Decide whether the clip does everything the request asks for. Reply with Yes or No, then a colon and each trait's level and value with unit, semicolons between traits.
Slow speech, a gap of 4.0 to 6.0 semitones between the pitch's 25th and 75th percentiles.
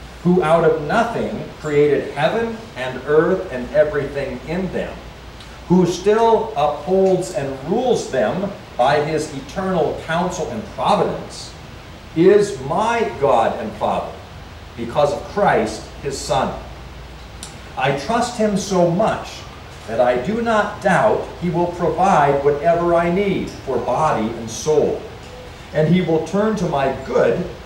Yes: slow, 130 wpm; average, 5.2 semitones